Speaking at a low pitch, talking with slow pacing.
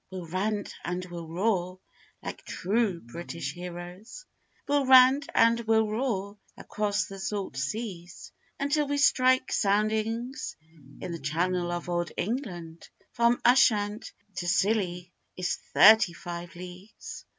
No: high, 195 Hz; slow, 125 wpm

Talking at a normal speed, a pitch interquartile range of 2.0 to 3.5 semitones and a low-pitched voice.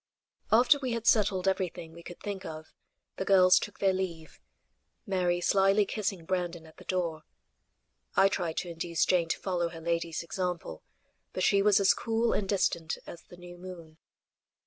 No: average, 170 wpm; narrow, 2.6 semitones; medium, 180 Hz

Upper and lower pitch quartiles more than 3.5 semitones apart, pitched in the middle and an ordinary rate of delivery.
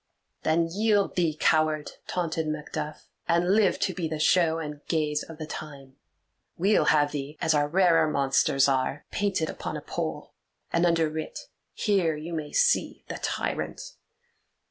No: average, 2.7 semitones; medium, 160 Hz; average, 150 wpm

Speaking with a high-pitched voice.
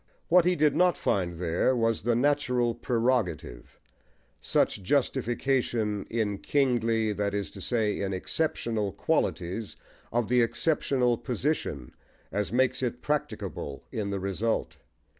No: low, 115 Hz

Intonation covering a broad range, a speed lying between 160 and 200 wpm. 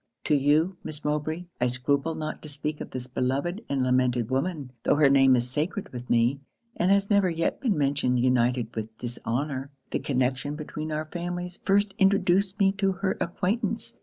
Yes: wide, 5.9 semitones; average, 180 wpm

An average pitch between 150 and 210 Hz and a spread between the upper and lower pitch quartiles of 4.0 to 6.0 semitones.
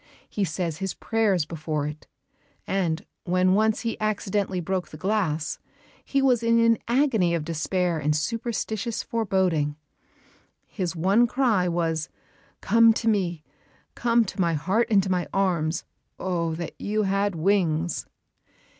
Yes: high, 190 Hz; average, 4.6 semitones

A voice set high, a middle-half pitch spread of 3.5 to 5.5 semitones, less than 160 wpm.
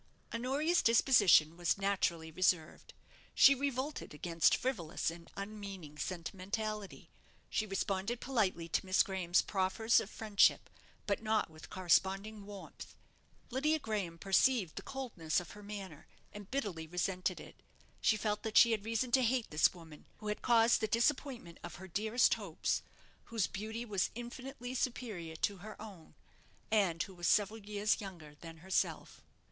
Yes: high, 205 Hz; average, 4.3 semitones; average, 150 wpm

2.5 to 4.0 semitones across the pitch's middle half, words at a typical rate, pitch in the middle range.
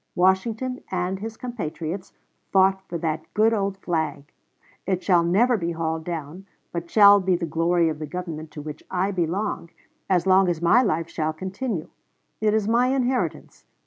Yes: average, 3.6 semitones; average, 170 wpm; medium, 180 Hz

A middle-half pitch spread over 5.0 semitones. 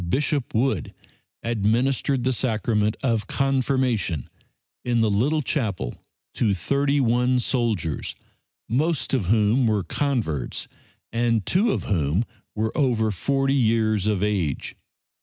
No: average, 4.3 semitones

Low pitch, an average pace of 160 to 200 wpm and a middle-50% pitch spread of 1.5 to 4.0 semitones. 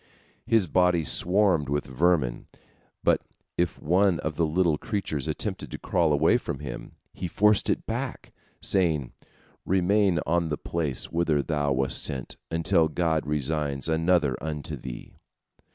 No: very low, 80 Hz; average, 140 wpm; average, 3.4 semitones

